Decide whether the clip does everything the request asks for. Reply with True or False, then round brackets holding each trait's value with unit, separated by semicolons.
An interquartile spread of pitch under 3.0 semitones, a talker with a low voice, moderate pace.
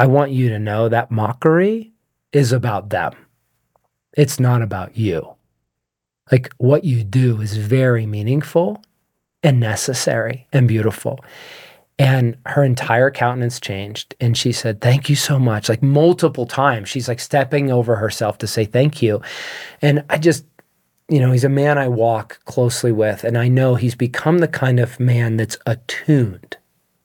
False (3.7 semitones; 125 Hz; 160 wpm)